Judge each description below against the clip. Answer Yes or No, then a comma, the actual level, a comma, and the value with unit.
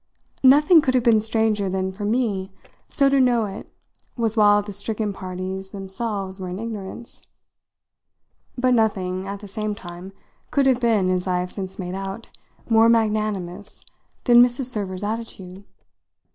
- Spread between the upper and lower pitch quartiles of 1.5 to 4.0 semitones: Yes, average, 3.3 semitones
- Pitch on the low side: No, high, 205 Hz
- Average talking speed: Yes, average, 155 wpm